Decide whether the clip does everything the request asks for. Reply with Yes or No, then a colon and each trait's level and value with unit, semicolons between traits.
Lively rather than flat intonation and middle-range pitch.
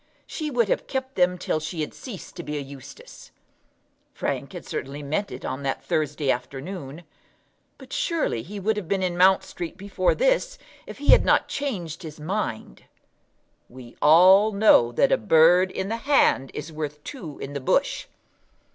Yes: wide, 5.9 semitones; medium, 175 Hz